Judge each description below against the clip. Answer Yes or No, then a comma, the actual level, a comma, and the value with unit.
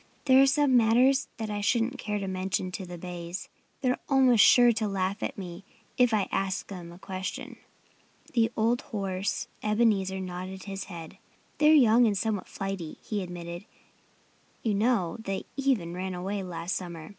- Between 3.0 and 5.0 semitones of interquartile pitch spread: Yes, average, 4.0 semitones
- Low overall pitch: No, high, 195 Hz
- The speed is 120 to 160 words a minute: No, average, 170 wpm